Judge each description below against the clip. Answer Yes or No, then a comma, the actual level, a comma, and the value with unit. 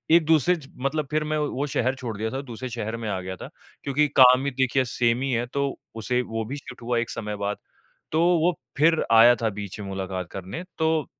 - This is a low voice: Yes, low, 125 Hz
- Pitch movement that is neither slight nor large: Yes, average, 4.1 semitones